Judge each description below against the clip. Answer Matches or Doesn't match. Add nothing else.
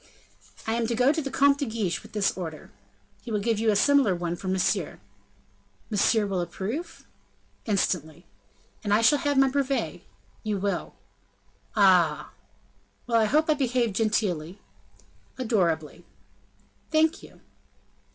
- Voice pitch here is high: Matches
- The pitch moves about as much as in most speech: Doesn't match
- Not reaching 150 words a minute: Matches